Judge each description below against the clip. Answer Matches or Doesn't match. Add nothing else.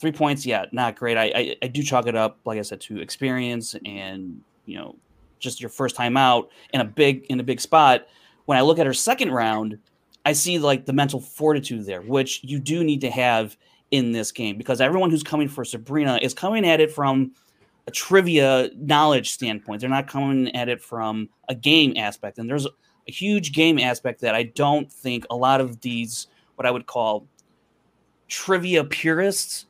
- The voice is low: Matches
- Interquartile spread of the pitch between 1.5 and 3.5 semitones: Doesn't match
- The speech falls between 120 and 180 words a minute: Doesn't match